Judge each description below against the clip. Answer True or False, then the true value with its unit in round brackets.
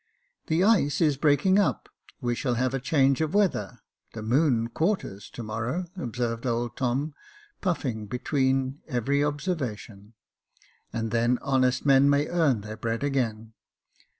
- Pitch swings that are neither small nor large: True (4.2 semitones)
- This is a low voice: True (130 Hz)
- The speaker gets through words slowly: False (155 wpm)